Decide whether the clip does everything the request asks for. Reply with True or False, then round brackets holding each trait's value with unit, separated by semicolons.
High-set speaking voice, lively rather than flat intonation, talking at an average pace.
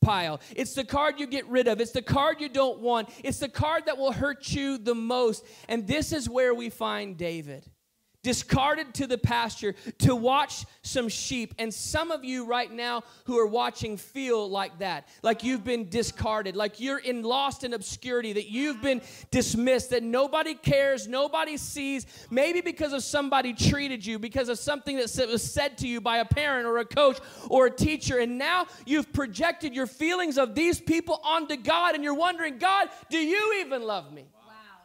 False (260 Hz; 3.8 semitones; 195 wpm)